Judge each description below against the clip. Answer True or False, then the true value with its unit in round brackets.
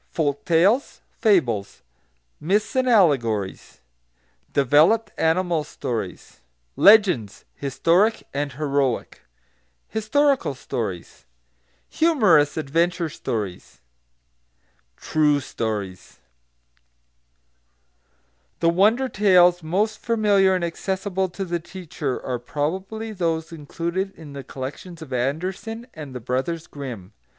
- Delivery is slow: True (95 wpm)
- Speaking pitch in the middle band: True (165 Hz)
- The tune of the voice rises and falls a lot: True (5.9 semitones)